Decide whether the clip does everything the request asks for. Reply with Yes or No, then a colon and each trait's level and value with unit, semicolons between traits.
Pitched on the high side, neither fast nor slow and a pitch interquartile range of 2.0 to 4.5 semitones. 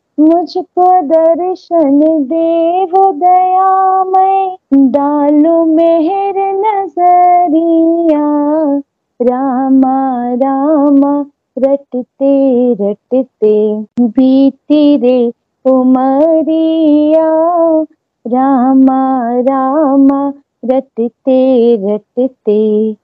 No: very high, 285 Hz; slow, 45 wpm; average, 4.2 semitones